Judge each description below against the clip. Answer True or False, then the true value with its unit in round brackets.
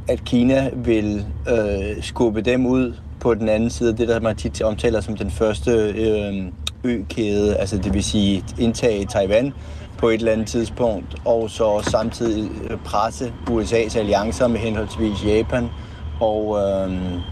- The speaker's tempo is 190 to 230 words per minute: False (150 wpm)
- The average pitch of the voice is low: True (110 Hz)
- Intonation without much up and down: True (2.3 semitones)